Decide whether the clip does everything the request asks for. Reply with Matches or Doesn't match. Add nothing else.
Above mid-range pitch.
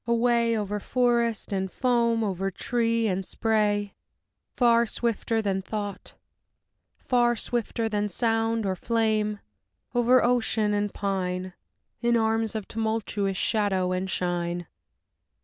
Matches